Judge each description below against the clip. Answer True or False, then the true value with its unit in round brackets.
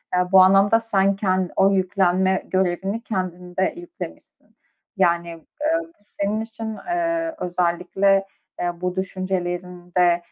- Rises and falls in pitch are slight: True (2.2 semitones)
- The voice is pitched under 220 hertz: True (190 Hz)